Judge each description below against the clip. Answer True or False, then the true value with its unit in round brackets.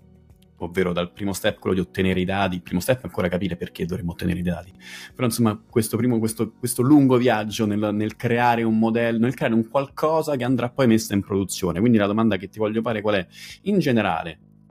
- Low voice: True (110 Hz)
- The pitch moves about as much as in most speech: True (4.1 semitones)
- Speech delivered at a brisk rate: True (220 wpm)